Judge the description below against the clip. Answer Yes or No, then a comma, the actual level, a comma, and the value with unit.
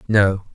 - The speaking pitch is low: Yes, low, 100 Hz